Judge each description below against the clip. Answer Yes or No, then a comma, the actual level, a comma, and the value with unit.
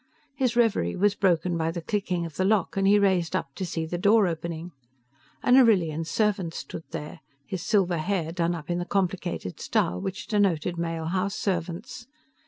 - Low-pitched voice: No, medium, 180 Hz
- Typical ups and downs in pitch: Yes, average, 3.3 semitones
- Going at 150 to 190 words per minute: Yes, average, 185 wpm